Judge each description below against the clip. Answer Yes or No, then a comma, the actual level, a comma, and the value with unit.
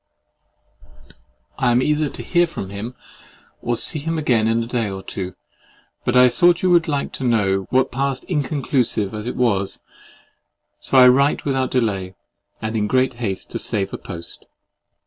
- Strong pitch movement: No, average, 4.8 semitones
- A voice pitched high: No, low, 125 Hz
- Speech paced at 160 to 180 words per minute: Yes, average, 165 wpm